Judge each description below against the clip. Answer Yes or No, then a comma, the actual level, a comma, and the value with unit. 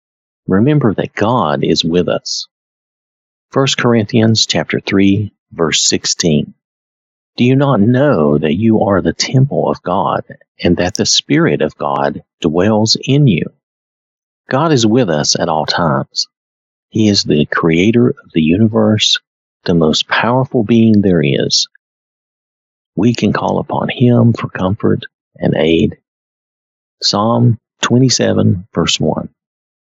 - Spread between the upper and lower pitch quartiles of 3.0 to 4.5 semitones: No, average, 5.3 semitones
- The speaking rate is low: Yes, slow, 130 wpm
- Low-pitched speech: Yes, low, 110 Hz